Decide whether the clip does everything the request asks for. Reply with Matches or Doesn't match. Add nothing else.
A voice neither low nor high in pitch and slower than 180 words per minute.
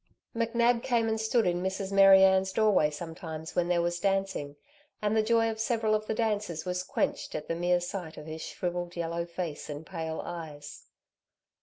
Doesn't match